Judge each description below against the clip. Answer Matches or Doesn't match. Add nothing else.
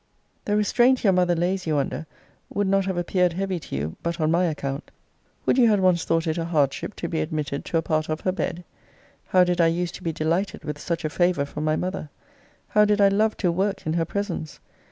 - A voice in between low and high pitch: Matches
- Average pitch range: Matches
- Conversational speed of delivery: Doesn't match